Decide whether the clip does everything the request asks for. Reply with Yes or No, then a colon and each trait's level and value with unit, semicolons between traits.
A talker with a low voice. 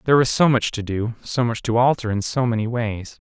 Yes: low, 115 Hz